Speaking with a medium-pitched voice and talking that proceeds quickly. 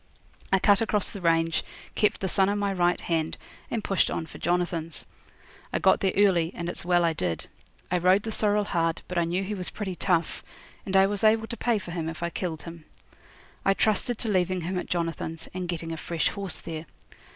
Yes: medium, 180 Hz; fast, 220 wpm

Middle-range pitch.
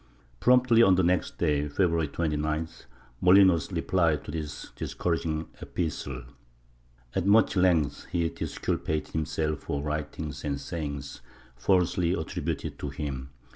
No: very low, 80 Hz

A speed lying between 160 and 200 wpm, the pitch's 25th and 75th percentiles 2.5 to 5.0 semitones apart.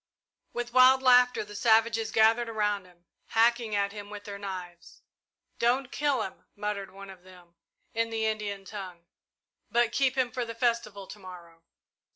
Yes: average, 165 wpm; average, 3.3 semitones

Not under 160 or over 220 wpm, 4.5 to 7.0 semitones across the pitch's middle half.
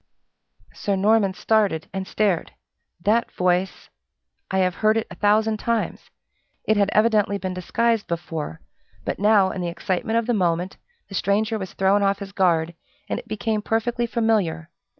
No: average, 165 wpm; average, 3.0 semitones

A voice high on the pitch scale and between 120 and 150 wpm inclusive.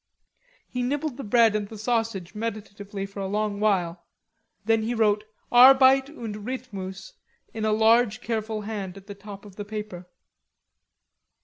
Yes: high, 215 Hz; average, 145 wpm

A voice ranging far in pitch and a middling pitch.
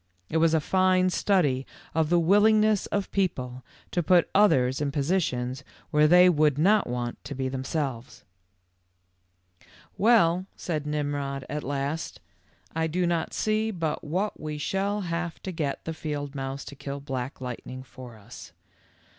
No: average, 4.9 semitones; medium, 155 Hz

